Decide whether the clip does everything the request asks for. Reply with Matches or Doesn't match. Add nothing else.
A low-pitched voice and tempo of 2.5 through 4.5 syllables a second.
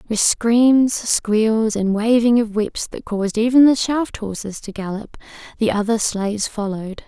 Doesn't match